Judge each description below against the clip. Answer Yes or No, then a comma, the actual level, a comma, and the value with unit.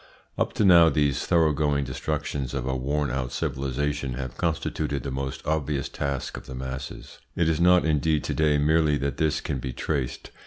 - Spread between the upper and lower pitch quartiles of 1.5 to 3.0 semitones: Yes, average, 2.7 semitones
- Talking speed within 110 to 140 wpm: No, average, 185 wpm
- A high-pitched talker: No, very low, 70 Hz